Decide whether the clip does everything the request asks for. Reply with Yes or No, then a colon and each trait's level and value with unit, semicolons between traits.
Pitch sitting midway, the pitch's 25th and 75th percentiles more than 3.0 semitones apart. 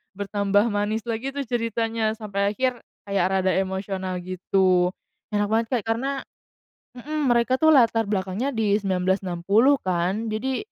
No: high, 210 Hz; average, 3.7 semitones